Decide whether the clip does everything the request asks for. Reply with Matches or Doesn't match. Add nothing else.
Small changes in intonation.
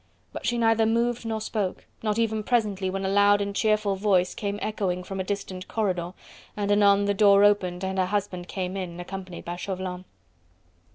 Matches